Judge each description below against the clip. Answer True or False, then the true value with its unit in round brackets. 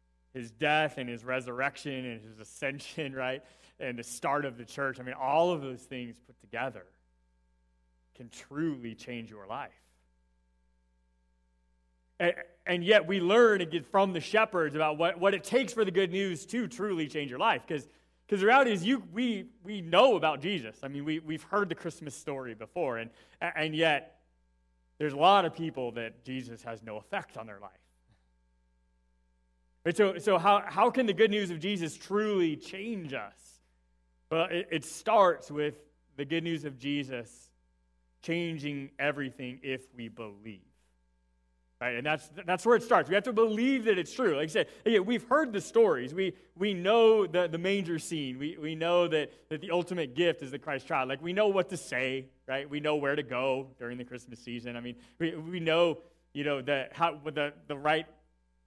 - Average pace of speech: True (185 wpm)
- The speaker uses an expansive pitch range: True (7.2 semitones)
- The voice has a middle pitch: True (145 Hz)